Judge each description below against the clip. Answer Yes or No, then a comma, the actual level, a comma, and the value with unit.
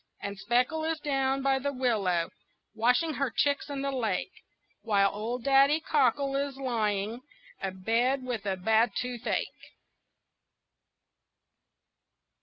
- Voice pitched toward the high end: Yes, very high, 250 Hz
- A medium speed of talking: No, slow, 115 wpm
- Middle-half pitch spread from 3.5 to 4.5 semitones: Yes, average, 4.0 semitones